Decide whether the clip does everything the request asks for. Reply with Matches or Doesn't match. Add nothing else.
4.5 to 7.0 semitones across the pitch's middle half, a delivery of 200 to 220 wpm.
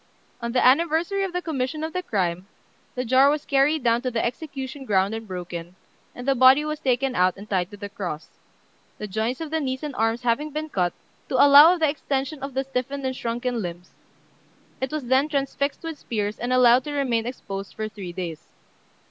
Matches